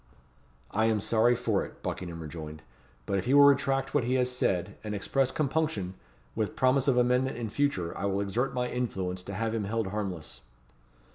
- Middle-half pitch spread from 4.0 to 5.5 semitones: Yes, average, 5.0 semitones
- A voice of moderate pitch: No, low, 115 Hz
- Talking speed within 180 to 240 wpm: Yes, average, 190 wpm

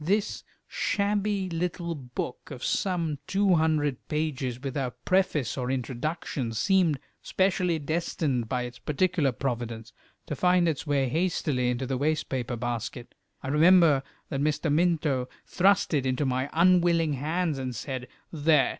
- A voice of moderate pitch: Yes, medium, 150 Hz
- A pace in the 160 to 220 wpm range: No, average, 140 wpm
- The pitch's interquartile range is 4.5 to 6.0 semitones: Yes, average, 5.0 semitones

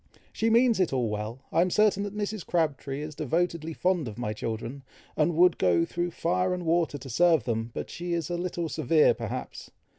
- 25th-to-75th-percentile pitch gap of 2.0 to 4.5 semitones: No, wide, 5.6 semitones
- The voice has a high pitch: No, medium, 165 Hz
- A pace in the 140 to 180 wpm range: No, fast, 205 wpm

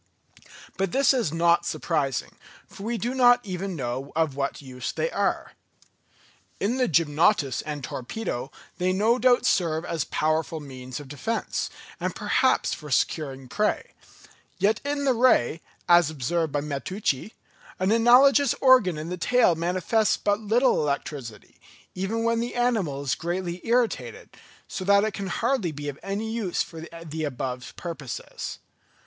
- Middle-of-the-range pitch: Yes, medium, 175 Hz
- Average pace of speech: Yes, average, 155 wpm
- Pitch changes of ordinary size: No, wide, 7.3 semitones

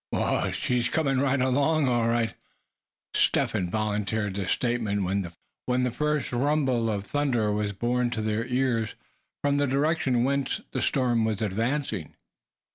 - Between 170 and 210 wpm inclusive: No, average, 145 wpm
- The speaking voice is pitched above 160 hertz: No, low, 120 Hz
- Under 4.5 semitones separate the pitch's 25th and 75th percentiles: Yes, average, 4.0 semitones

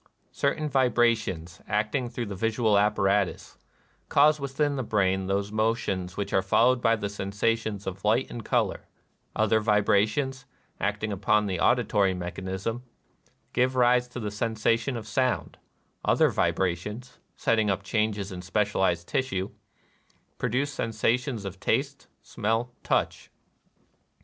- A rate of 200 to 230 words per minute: No, slow, 135 wpm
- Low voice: Yes, low, 110 Hz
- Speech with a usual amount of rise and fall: Yes, average, 3.7 semitones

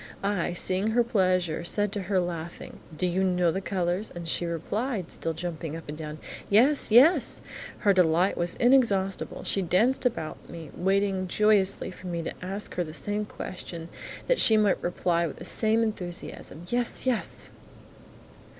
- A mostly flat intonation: No, average, 3.6 semitones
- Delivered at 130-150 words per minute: No, average, 165 wpm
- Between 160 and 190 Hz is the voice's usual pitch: Yes, medium, 185 Hz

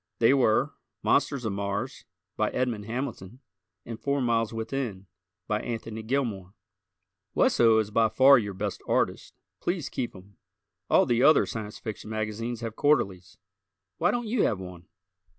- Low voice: Yes, low, 115 Hz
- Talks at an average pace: Yes, average, 150 wpm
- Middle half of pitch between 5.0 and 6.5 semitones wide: No, average, 3.4 semitones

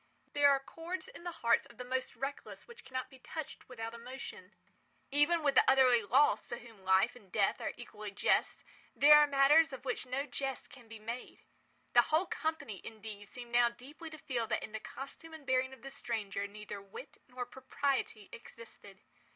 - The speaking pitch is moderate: No, very high, 255 Hz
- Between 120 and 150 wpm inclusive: No, average, 190 wpm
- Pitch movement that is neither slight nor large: Yes, average, 3.8 semitones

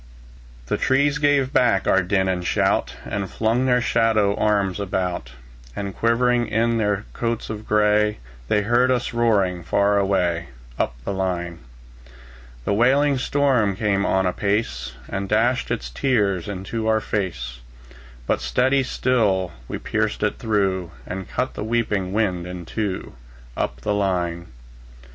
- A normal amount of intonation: Yes, average, 3.8 semitones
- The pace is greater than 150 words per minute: No, average, 145 wpm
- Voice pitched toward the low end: Yes, low, 105 Hz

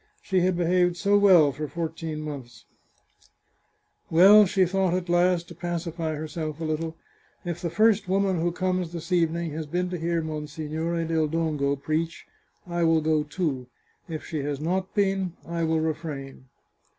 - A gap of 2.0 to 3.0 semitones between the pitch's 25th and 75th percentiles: Yes, narrow, 2.4 semitones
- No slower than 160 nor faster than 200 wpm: Yes, average, 175 wpm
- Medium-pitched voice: Yes, medium, 165 Hz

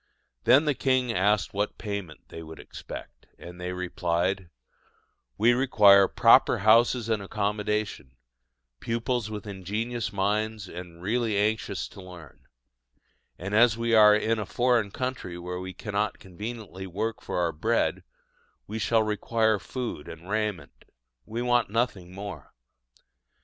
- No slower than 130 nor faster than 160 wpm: Yes, slow, 135 wpm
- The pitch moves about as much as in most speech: Yes, average, 3.6 semitones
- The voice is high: No, low, 105 Hz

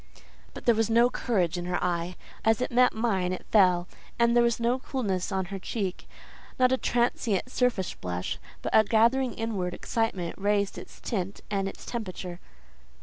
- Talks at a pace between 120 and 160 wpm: No, average, 170 wpm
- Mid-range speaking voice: No, high, 210 Hz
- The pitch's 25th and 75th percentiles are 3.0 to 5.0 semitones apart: Yes, average, 4.4 semitones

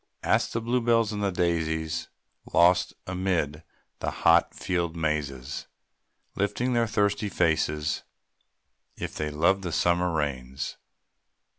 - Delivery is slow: Yes, slow, 125 wpm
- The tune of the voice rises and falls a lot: No, average, 4.7 semitones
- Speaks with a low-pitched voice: Yes, very low, 85 Hz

